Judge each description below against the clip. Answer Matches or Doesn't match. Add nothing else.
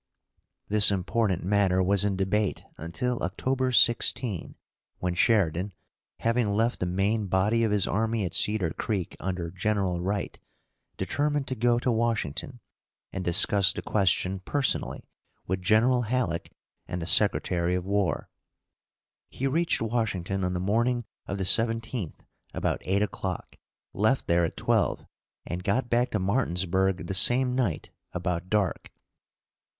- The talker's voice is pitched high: Doesn't match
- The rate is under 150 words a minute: Matches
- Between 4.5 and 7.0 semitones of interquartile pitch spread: Doesn't match